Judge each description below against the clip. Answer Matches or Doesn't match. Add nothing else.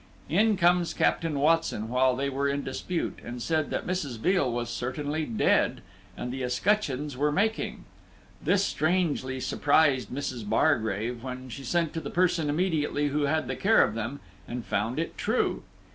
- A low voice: Doesn't match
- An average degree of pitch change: Matches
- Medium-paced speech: Matches